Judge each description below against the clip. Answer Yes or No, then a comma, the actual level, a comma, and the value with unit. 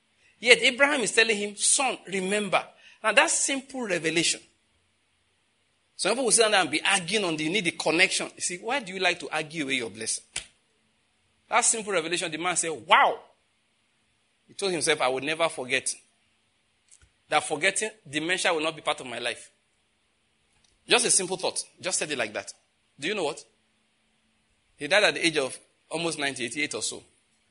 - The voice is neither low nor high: Yes, medium, 160 Hz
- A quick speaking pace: No, average, 180 wpm